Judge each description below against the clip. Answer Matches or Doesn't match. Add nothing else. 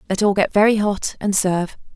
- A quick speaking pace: Matches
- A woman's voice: Matches